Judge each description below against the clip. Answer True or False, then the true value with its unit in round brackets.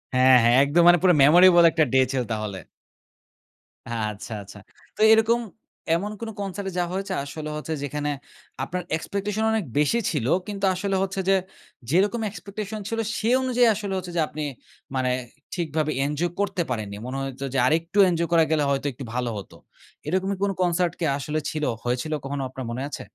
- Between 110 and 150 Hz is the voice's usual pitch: False (165 Hz)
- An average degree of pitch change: False (6.0 semitones)